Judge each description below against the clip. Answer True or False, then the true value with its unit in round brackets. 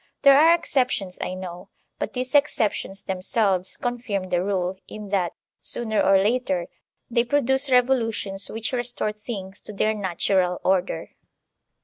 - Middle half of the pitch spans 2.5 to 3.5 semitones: False (4.6 semitones)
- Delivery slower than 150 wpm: True (135 wpm)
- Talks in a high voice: True (210 Hz)